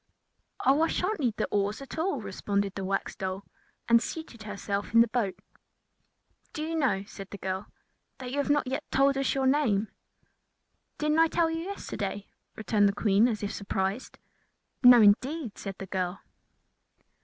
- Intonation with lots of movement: Yes, wide, 6.0 semitones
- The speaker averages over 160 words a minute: Yes, average, 175 wpm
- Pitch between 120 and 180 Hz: No, high, 230 Hz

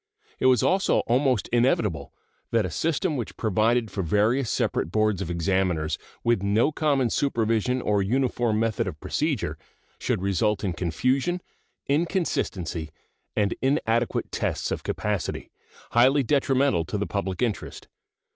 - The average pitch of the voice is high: No, low, 115 Hz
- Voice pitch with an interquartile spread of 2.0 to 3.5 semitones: No, average, 5.1 semitones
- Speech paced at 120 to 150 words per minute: Yes, slow, 135 wpm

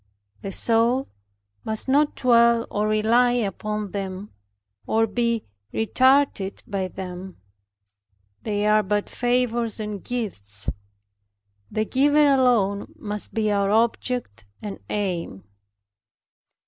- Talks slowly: Yes, slow, 105 wpm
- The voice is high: Yes, high, 215 Hz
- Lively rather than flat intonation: No, average, 3.2 semitones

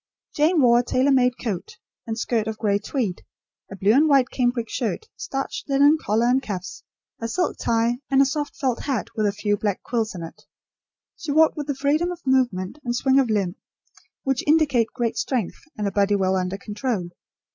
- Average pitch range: Yes, average, 4.7 semitones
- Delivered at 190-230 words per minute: Yes, average, 200 wpm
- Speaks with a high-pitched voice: Yes, high, 240 Hz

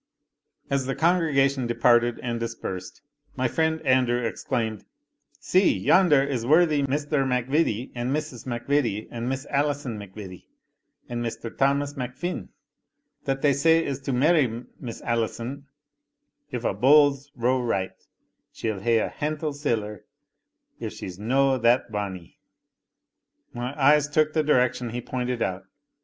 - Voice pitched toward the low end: Yes, low, 130 Hz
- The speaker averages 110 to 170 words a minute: Yes, slow, 135 wpm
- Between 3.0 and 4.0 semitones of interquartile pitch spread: Yes, average, 3.5 semitones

